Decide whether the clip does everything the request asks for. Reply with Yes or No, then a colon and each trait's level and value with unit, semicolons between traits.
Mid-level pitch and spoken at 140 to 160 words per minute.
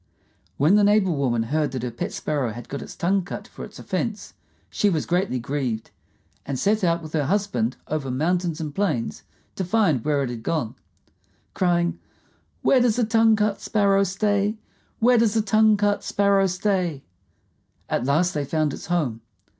No: medium, 175 Hz; average, 180 wpm